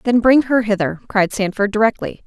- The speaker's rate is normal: Yes, average, 185 wpm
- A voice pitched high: Yes, high, 215 Hz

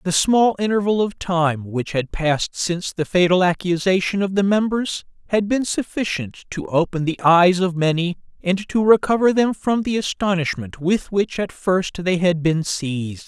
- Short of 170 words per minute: No, average, 175 wpm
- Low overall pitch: No, medium, 185 Hz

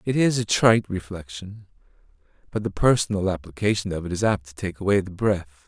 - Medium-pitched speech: No, low, 100 Hz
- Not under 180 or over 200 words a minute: Yes, average, 190 wpm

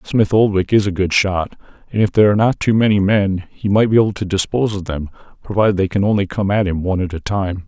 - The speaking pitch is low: Yes, low, 100 Hz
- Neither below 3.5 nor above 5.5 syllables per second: No, 6.4 syllables/s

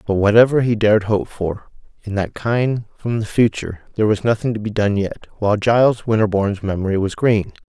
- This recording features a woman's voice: No, male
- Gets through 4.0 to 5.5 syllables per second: No, 5.8 syllables/s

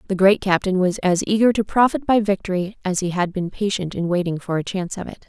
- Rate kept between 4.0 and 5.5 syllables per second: No, 6.1 syllables/s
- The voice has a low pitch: No, high, 190 Hz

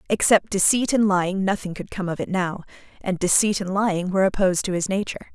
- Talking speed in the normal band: No, fast, 215 wpm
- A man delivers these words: No, female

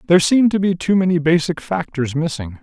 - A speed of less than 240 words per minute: Yes, fast, 205 wpm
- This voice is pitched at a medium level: Yes, medium, 165 Hz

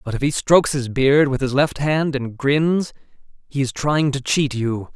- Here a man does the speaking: Yes, male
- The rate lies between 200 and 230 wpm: Yes, fast, 205 wpm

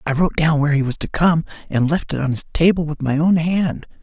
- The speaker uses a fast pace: Yes, fast, 270 wpm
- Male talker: Yes, male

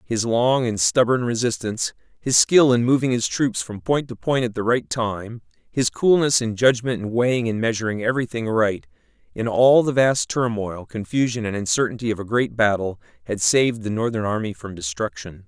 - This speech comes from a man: Yes, male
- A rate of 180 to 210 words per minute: Yes, average, 185 wpm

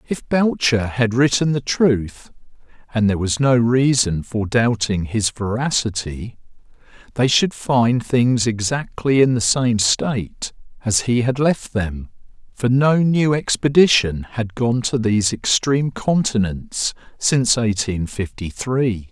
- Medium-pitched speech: No, low, 120 Hz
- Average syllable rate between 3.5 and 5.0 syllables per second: Yes, 3.9 syllables/s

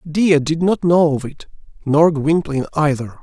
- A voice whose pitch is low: No, medium, 155 Hz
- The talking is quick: No, average, 165 wpm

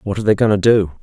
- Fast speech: Yes, fast, 350 wpm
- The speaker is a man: Yes, male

